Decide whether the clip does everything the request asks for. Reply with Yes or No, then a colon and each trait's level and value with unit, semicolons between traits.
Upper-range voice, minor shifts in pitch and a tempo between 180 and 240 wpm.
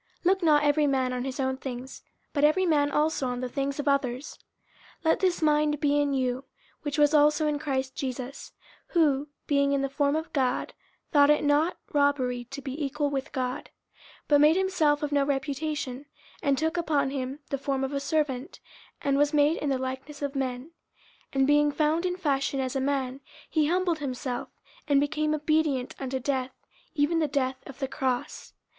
Yes: very high, 285 Hz; narrow, 2.1 semitones; average, 200 wpm